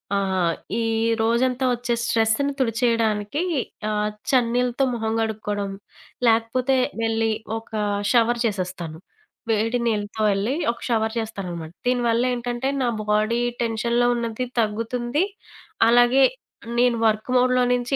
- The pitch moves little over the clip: Yes, narrow, 2.2 semitones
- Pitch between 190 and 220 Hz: No, high, 230 Hz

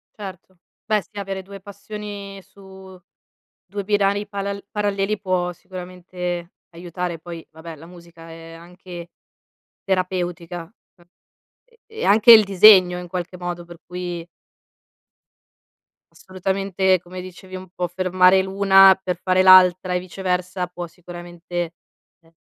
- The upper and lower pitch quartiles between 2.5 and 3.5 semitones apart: No, narrow, 1.8 semitones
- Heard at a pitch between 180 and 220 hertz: Yes, medium, 185 Hz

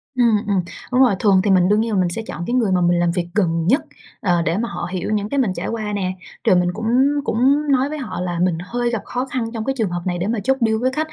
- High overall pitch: Yes, high, 210 Hz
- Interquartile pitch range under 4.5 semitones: No, average, 5.2 semitones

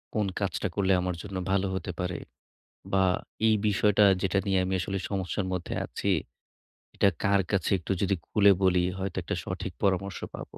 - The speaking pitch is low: Yes, very low, 95 Hz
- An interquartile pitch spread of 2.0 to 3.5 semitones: No, narrow, 1.4 semitones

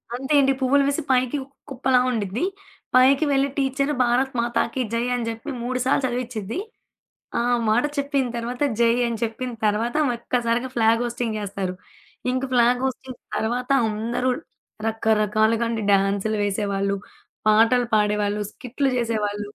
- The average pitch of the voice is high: Yes, high, 235 Hz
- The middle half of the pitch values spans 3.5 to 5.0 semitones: No, average, 3.0 semitones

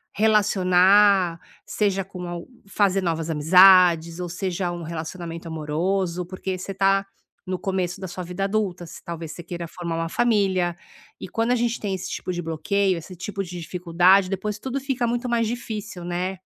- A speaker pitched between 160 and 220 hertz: Yes, medium, 185 Hz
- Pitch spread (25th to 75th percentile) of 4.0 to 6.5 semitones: No, narrow, 2.6 semitones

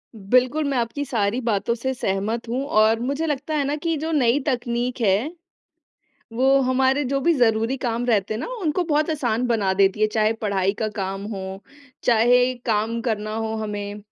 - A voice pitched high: Yes, high, 235 Hz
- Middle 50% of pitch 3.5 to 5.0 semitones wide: Yes, average, 3.8 semitones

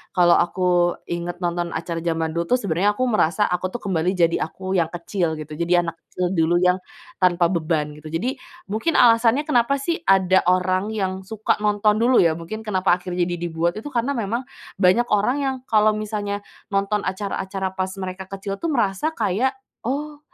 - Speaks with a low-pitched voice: No, high, 190 Hz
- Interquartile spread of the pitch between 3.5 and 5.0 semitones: Yes, average, 3.8 semitones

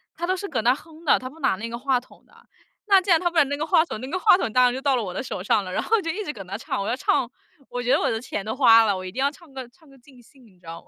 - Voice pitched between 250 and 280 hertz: Yes, very high, 260 Hz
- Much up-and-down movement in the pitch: Yes, wide, 6.0 semitones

